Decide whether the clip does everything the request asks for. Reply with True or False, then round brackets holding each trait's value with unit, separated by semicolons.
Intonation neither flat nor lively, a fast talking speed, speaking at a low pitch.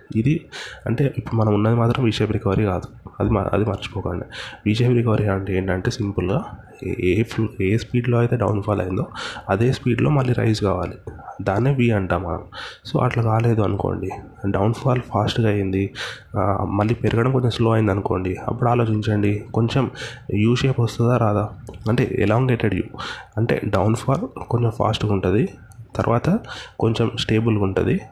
True (3.0 semitones; 140 wpm; 110 Hz)